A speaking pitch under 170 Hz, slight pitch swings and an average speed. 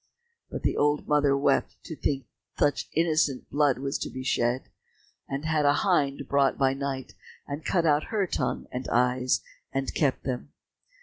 Yes: medium, 140 Hz; narrow, 2.0 semitones; average, 170 wpm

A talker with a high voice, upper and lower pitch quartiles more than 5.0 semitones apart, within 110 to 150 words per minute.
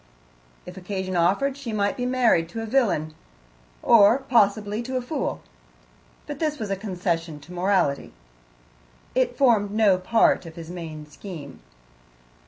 Yes: high, 200 Hz; wide, 5.5 semitones; average, 145 wpm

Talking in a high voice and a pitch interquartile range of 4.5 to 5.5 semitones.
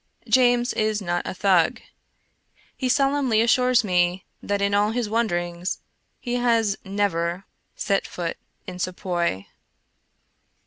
Yes: high, 205 Hz; average, 5.1 semitones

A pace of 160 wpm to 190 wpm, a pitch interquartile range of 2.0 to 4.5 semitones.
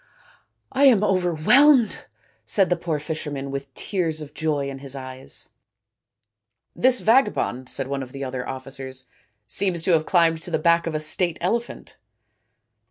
No: average, 165 wpm; average, 5.1 semitones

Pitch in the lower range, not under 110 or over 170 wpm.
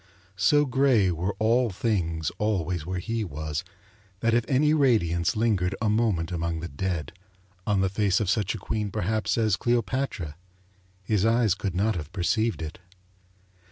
Yes: low, 100 Hz; average, 160 wpm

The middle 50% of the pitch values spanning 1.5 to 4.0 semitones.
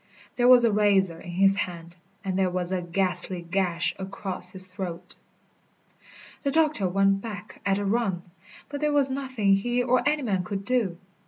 No: average, 4.8 semitones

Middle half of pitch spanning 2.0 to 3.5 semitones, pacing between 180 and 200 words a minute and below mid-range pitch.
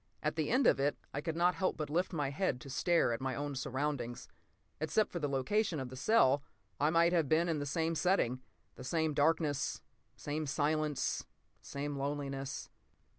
No: average, 3.2 semitones; average, 185 wpm; medium, 150 Hz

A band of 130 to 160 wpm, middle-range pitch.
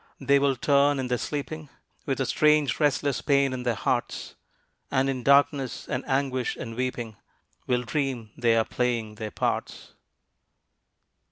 No: average, 150 wpm; low, 130 Hz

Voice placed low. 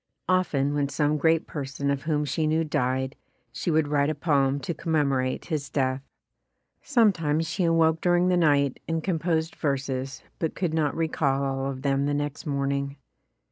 No: medium, 145 Hz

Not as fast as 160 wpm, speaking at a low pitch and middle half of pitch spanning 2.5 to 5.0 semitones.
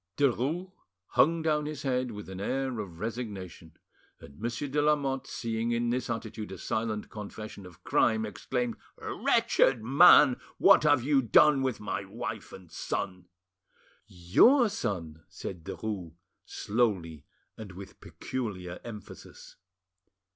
No: slow, 135 wpm; low, 115 Hz; wide, 5.5 semitones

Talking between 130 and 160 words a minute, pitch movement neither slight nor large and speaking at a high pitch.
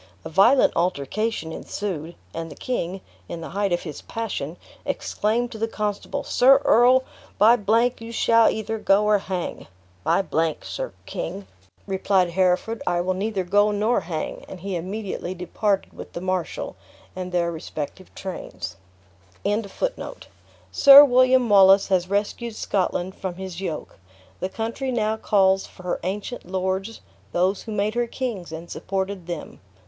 Yes: average, 150 wpm; average, 3.7 semitones; high, 195 Hz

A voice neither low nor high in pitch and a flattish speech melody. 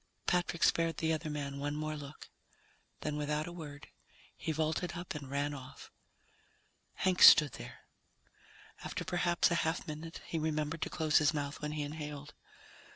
Yes: medium, 155 Hz; narrow, 2.0 semitones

